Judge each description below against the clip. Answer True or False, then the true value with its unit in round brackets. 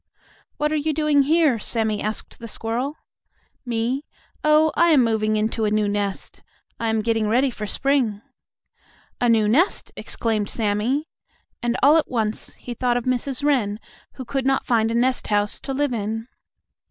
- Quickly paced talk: False (170 wpm)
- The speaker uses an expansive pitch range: False (4.2 semitones)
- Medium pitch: False (235 Hz)